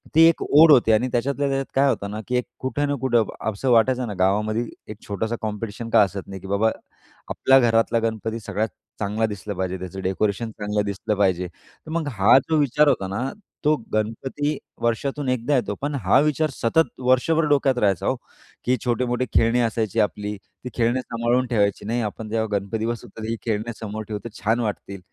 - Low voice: Yes, low, 115 Hz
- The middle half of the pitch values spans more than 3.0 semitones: Yes, average, 3.7 semitones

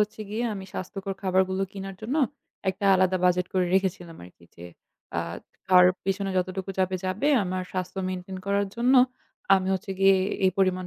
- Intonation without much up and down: Yes, narrow, 1.0 semitones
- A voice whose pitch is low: No, high, 190 Hz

